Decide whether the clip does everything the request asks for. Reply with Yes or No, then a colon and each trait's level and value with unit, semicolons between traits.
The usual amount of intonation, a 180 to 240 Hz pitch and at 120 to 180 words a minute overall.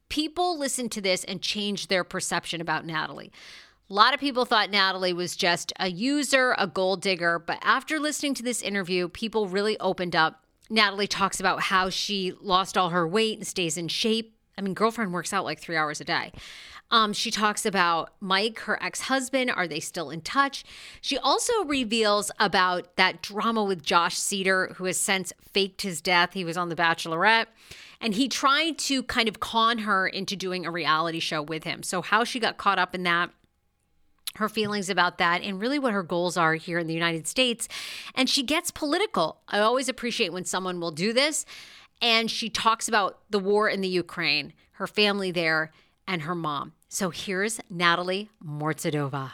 No: average, 4.4 semitones; high, 190 Hz; average, 190 wpm